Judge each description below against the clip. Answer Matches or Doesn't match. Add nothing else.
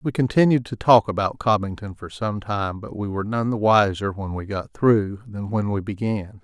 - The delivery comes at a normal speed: Doesn't match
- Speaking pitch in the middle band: Doesn't match